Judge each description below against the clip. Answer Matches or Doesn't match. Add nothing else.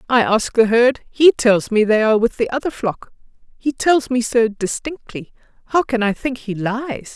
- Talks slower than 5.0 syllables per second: Matches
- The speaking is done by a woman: Matches